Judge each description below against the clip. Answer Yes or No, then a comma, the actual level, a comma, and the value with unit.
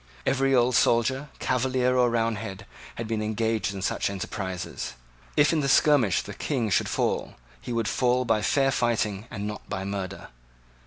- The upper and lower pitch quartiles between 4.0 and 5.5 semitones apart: No, average, 3.6 semitones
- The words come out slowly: No, average, 165 wpm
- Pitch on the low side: Yes, low, 115 Hz